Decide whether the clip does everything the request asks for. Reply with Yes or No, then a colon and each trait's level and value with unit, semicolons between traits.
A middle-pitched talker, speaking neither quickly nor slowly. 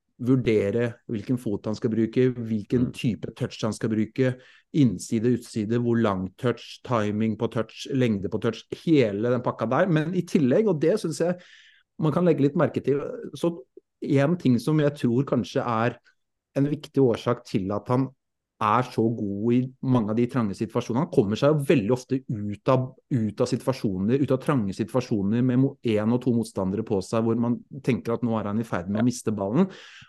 No: low, 120 Hz; average, 190 wpm